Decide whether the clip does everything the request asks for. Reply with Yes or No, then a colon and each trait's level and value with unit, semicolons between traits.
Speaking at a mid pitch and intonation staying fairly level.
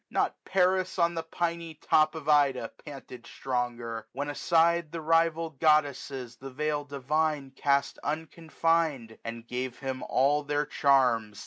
No: medium, 145 Hz; average, 3.8 semitones